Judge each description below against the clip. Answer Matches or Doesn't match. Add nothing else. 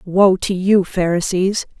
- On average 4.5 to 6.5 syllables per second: Doesn't match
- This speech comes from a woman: Matches